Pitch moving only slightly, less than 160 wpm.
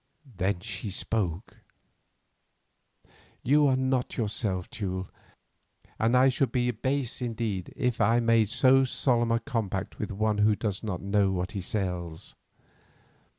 No: average, 4.0 semitones; slow, 135 wpm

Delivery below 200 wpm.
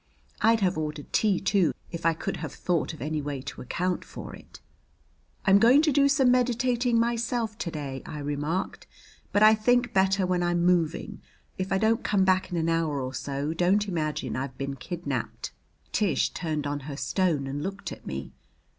Yes: average, 190 wpm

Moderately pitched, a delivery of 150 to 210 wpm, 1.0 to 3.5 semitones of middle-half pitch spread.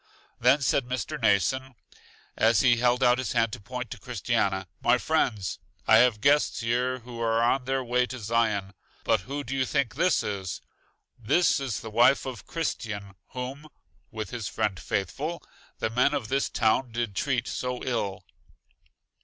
No: low, 120 Hz; average, 170 wpm; average, 3.0 semitones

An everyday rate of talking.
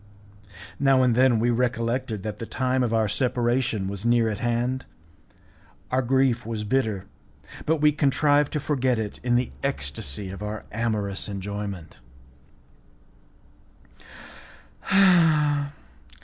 No: slow, 120 wpm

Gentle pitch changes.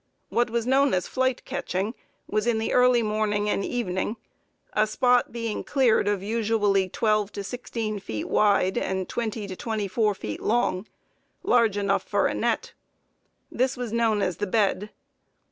No: average, 3.0 semitones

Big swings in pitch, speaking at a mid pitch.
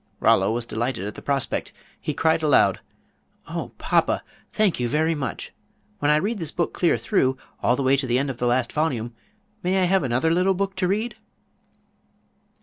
Yes: wide, 6.4 semitones; medium, 145 Hz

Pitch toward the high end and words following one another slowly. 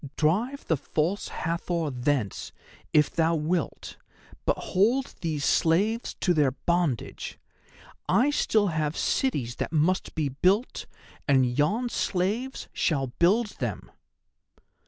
No: medium, 165 Hz; slow, 115 wpm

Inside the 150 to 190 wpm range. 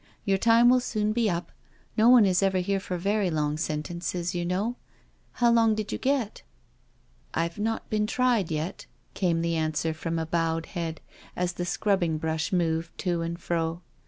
Yes: average, 180 wpm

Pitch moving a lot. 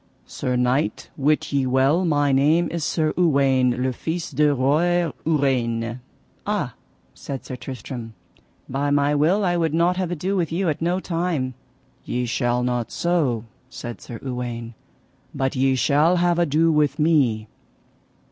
No: average, 4.7 semitones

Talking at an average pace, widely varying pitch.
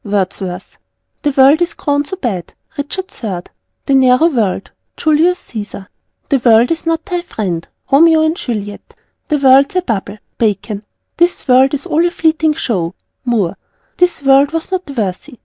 Yes: average, 160 wpm; wide, 7.4 semitones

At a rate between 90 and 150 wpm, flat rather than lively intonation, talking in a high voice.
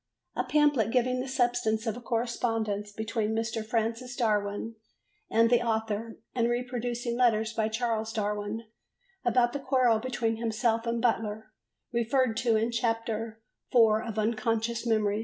Yes: average, 140 wpm; narrow, 1.6 semitones; high, 230 Hz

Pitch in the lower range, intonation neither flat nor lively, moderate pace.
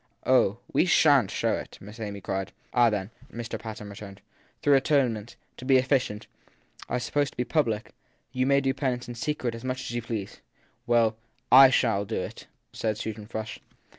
Yes: low, 120 Hz; average, 3.5 semitones; average, 185 wpm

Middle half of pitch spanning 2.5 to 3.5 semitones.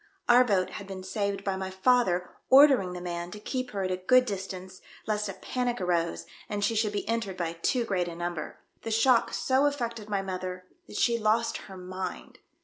No: average, 4.0 semitones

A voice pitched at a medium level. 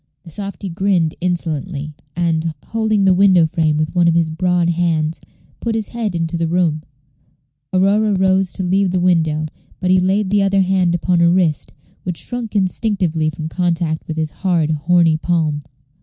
Yes: medium, 175 Hz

